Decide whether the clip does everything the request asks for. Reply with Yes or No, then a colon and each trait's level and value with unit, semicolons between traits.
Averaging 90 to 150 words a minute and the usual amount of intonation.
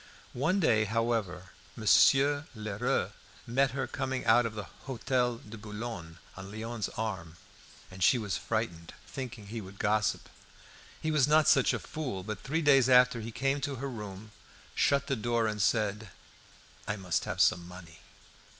No: average, 160 wpm; average, 4.4 semitones